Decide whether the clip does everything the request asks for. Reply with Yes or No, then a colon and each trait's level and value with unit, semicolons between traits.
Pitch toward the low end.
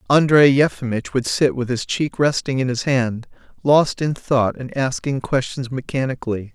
Yes: low, 130 Hz